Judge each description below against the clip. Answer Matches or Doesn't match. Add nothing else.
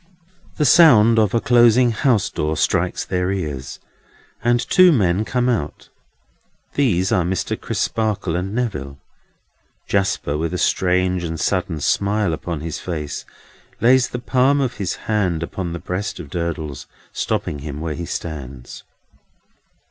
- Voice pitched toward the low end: Matches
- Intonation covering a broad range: Matches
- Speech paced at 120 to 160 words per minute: Matches